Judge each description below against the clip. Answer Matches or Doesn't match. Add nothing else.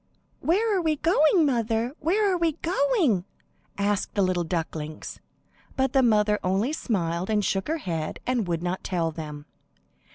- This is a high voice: Matches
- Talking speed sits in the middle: Matches